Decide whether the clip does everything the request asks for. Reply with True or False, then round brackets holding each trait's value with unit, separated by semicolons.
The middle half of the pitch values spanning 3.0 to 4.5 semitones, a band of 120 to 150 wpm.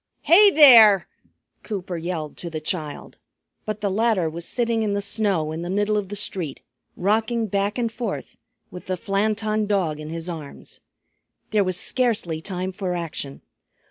False (4.1 semitones; 165 wpm)